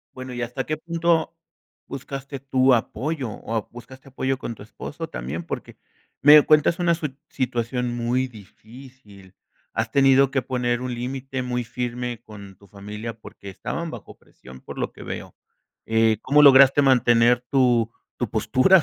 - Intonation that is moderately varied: Yes, average, 3.1 semitones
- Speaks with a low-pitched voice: Yes, low, 125 Hz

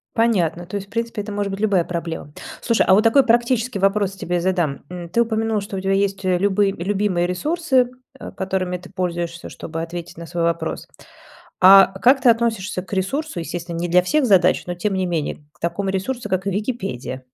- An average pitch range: Yes, average, 3.7 semitones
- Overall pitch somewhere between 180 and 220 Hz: Yes, high, 190 Hz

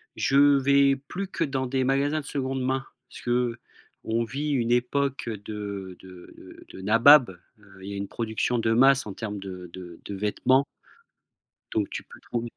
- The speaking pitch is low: Yes, low, 120 Hz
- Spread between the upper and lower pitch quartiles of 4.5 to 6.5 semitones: Yes, average, 5.1 semitones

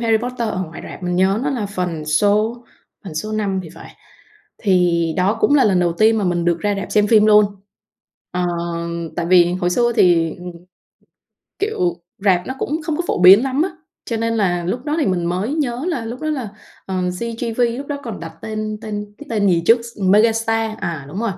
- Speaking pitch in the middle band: No, high, 210 Hz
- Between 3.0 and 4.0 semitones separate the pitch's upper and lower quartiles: No, average, 4.4 semitones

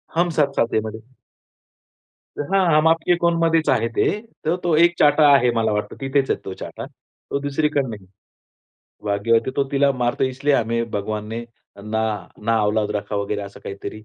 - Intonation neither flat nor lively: No, wide, 5.8 semitones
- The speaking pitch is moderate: No, low, 130 Hz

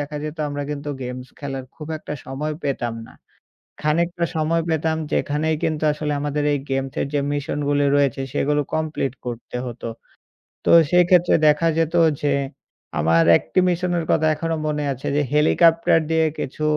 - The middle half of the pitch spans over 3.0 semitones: No, narrow, 2.4 semitones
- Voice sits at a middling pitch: Yes, medium, 150 Hz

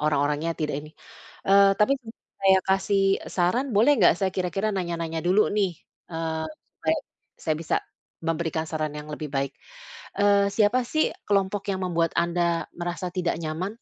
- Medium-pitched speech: Yes, medium, 175 Hz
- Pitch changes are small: No, average, 3.5 semitones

